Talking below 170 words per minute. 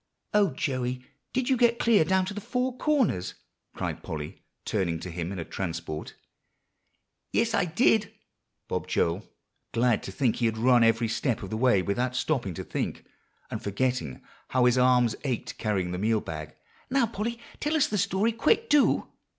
No: average, 175 wpm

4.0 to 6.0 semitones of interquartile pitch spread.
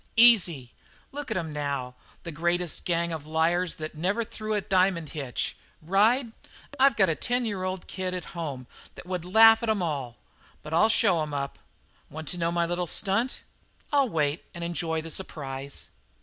Yes: average, 4.4 semitones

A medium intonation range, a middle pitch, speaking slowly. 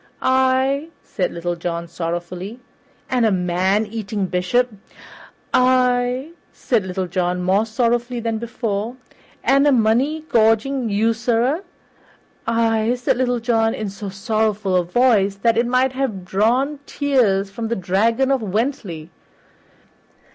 No: average, 4.4 semitones; high, 225 Hz; slow, 125 wpm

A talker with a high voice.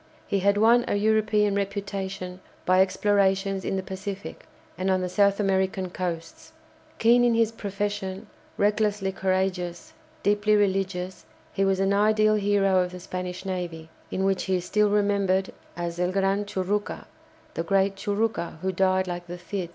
Yes: high, 195 Hz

